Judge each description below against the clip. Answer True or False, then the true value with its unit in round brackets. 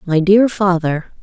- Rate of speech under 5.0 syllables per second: True (3.9 syllables/s)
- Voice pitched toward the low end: False (185 Hz)